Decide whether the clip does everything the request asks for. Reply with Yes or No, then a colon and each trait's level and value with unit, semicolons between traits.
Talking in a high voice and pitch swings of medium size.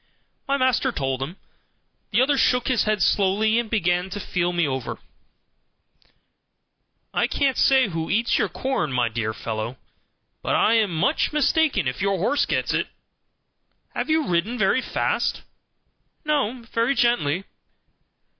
No: high, 210 Hz; wide, 7.2 semitones